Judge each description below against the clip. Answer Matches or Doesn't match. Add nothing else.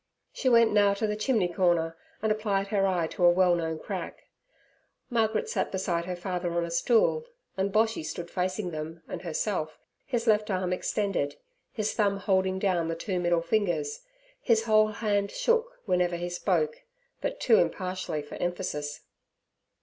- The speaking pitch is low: Doesn't match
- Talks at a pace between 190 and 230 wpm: Doesn't match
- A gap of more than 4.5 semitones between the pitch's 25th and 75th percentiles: Doesn't match